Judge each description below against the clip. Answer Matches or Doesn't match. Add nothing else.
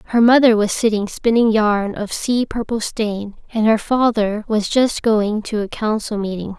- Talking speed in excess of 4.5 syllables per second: Doesn't match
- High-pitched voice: Matches